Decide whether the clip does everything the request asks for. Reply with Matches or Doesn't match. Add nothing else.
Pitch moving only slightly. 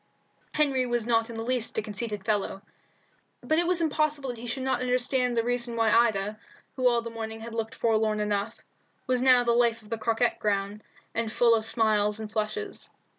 Matches